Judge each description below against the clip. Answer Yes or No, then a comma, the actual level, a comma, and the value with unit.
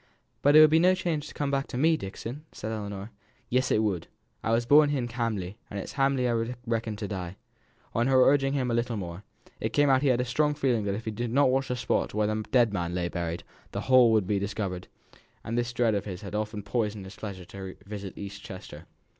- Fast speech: Yes, fast, 255 wpm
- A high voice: No, low, 115 Hz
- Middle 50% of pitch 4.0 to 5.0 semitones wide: Yes, average, 4.5 semitones